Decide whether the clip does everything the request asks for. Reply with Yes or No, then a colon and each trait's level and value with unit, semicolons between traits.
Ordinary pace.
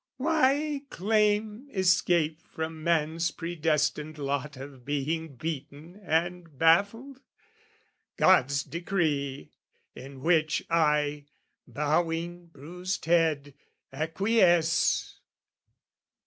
No: slow, 75 wpm